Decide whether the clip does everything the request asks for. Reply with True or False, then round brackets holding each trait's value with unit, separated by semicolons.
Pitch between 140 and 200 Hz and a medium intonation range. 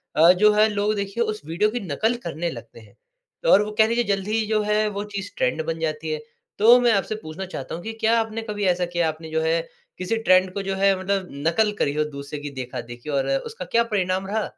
True (190 Hz; 5.0 semitones)